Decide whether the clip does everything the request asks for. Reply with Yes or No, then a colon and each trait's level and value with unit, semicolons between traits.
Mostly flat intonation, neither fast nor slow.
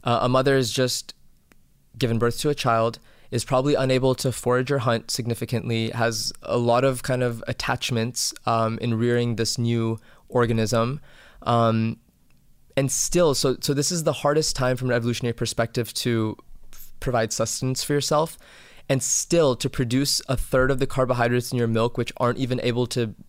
Yes: narrow, 2.3 semitones; average, 175 wpm